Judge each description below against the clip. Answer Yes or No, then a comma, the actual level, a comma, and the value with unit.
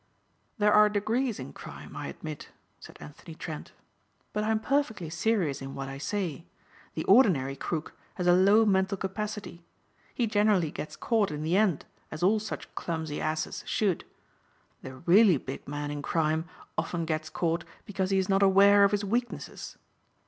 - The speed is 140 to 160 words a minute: No, average, 170 wpm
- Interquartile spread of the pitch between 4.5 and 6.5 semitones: Yes, average, 5.0 semitones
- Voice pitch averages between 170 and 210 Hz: Yes, medium, 185 Hz